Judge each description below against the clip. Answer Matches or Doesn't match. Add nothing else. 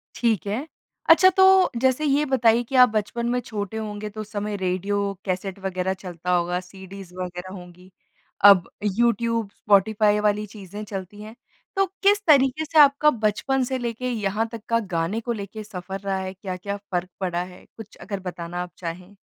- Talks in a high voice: Matches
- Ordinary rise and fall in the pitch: Matches